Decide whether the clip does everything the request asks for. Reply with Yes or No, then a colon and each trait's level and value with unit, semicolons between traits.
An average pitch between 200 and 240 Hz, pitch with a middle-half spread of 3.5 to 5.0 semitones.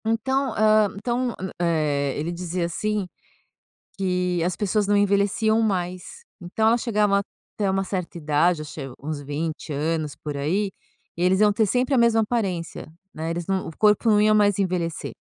No: high, 190 Hz; average, 4.2 semitones